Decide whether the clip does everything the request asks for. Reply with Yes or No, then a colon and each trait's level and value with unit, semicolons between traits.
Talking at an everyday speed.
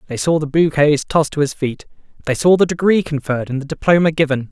No: fast, 225 wpm